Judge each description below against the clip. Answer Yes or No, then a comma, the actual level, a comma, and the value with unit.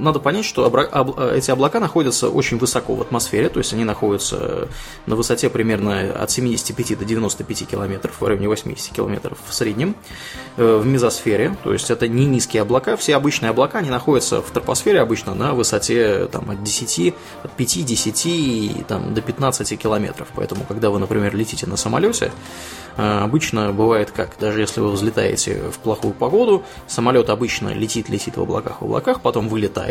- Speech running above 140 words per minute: Yes, fast, 160 wpm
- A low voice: Yes, low, 110 Hz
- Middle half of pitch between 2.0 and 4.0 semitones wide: Yes, average, 3.3 semitones